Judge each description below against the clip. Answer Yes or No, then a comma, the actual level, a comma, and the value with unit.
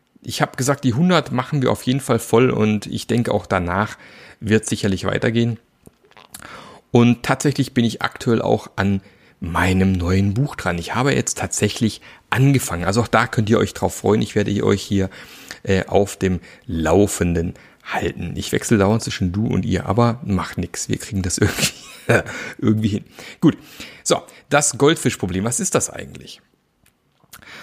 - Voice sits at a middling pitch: No, low, 105 Hz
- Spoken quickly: No, average, 165 wpm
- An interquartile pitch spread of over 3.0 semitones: Yes, average, 4.0 semitones